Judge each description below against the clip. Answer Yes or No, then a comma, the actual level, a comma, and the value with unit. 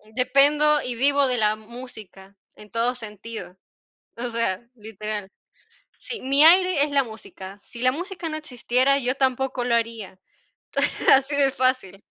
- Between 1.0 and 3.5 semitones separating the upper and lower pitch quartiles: No, average, 4.1 semitones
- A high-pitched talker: Yes, very high, 250 Hz